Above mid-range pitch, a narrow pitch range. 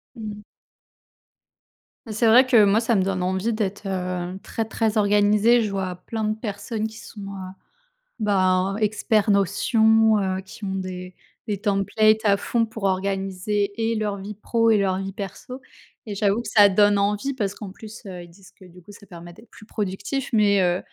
Yes: high, 205 Hz; narrow, 2.3 semitones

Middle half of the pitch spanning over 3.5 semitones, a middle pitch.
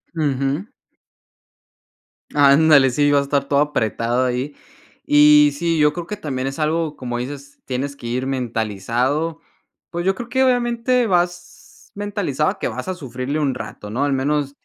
Yes: average, 4.1 semitones; medium, 145 Hz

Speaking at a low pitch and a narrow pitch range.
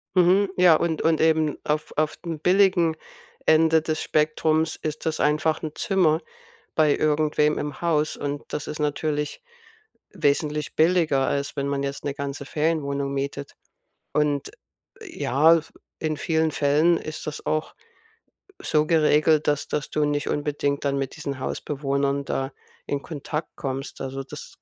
No: medium, 150 Hz; narrow, 2.0 semitones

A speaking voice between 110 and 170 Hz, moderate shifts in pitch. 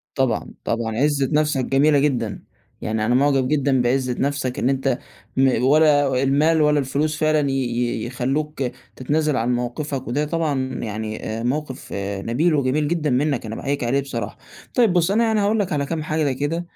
Yes: medium, 140 Hz; average, 3.3 semitones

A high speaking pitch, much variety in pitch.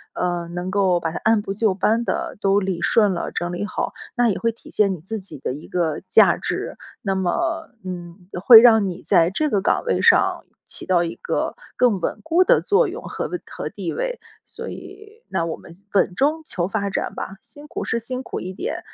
Yes: high, 200 Hz; wide, 5.9 semitones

